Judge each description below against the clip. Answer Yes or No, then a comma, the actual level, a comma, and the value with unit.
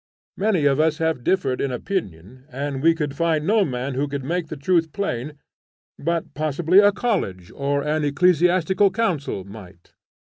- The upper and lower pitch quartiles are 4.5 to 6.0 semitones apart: Yes, average, 4.8 semitones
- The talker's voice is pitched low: No, medium, 150 Hz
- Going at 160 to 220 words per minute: Yes, average, 165 wpm